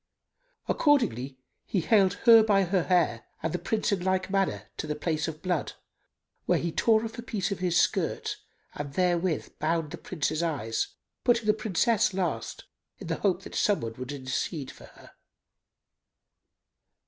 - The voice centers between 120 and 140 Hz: No, medium, 180 Hz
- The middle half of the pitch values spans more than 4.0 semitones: Yes, average, 4.5 semitones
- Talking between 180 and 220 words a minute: No, average, 165 wpm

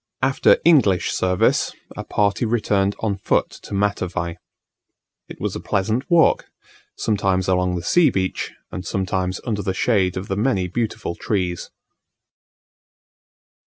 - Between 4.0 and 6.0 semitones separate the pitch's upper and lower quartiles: No, average, 3.1 semitones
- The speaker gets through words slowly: Yes, slow, 130 wpm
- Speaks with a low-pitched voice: Yes, low, 100 Hz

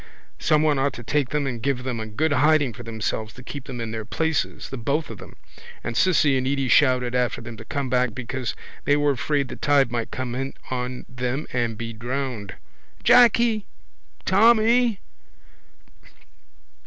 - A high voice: No, low, 130 Hz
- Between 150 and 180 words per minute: Yes, average, 175 wpm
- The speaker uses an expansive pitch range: No, average, 3.5 semitones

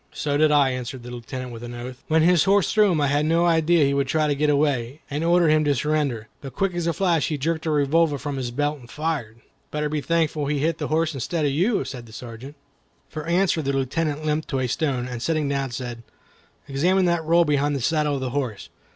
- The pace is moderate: No, fast, 245 wpm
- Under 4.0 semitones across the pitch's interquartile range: Yes, average, 3.3 semitones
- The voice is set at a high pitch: No, medium, 150 Hz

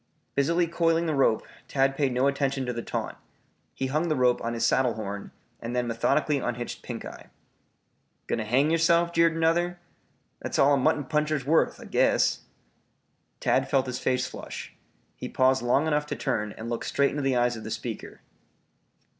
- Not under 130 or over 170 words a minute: No, average, 180 wpm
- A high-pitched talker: No, low, 135 Hz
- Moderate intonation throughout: Yes, average, 4.0 semitones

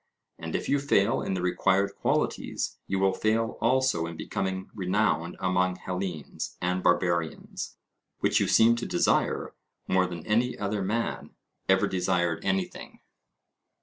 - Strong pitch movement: No, average, 2.9 semitones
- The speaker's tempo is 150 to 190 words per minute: No, average, 140 wpm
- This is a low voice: Yes, very low, 95 Hz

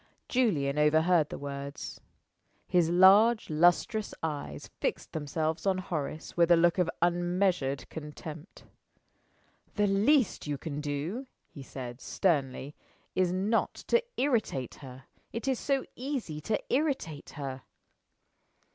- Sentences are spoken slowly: Yes, slow, 120 wpm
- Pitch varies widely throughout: Yes, wide, 5.7 semitones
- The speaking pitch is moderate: Yes, medium, 170 Hz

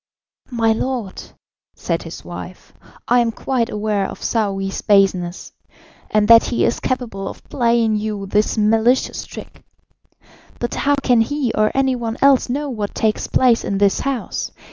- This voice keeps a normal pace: Yes, average, 155 wpm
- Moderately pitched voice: No, high, 225 Hz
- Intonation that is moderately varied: Yes, average, 3.0 semitones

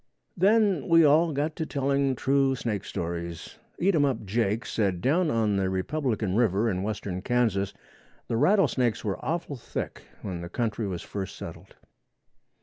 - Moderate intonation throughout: No, wide, 6.8 semitones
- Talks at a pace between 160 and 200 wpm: No, average, 150 wpm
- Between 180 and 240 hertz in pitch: No, low, 120 Hz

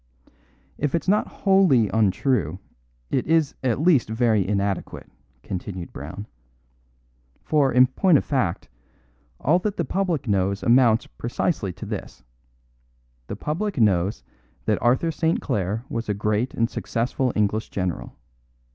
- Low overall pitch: Yes, low, 120 Hz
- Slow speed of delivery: Yes, slow, 130 wpm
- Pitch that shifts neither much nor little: No, wide, 6.6 semitones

